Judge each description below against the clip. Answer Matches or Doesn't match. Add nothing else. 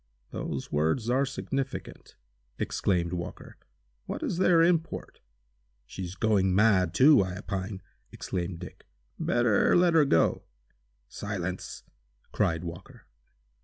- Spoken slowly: Matches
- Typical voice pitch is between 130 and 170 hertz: Doesn't match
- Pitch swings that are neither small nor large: Doesn't match